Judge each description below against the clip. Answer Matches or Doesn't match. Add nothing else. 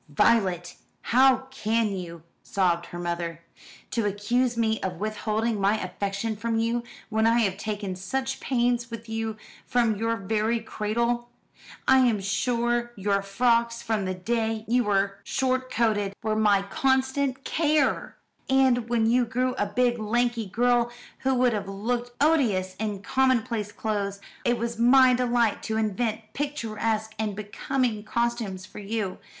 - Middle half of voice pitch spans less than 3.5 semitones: Matches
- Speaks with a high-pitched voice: Matches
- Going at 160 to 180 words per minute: Doesn't match